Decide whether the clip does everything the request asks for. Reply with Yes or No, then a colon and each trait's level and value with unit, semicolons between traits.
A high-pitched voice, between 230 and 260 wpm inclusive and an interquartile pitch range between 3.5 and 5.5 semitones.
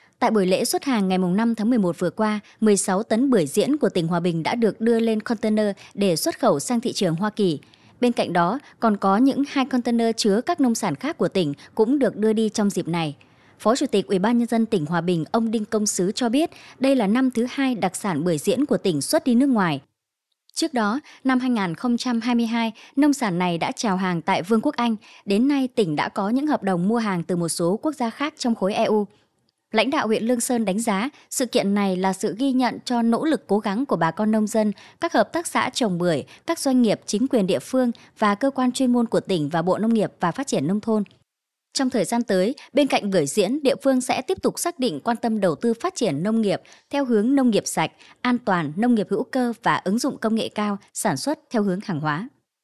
Yes: high, 225 Hz; average, 245 wpm; average, 4.6 semitones